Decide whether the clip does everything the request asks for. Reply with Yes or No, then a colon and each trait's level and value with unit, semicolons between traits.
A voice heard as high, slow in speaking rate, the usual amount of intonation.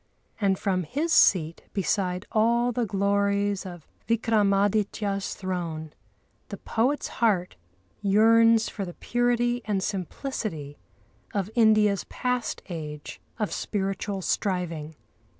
Yes: high, 200 Hz; slow, 105 wpm; average, 3.6 semitones